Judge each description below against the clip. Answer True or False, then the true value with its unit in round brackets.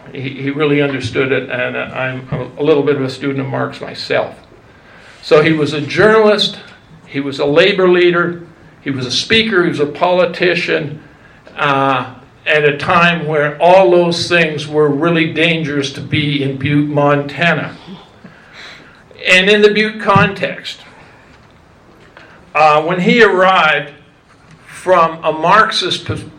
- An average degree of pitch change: True (3.5 semitones)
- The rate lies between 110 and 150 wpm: True (140 wpm)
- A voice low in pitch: False (155 Hz)